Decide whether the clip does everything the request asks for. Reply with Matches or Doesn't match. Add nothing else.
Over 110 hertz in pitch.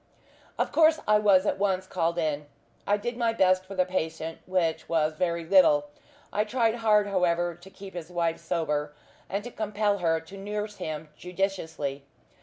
Matches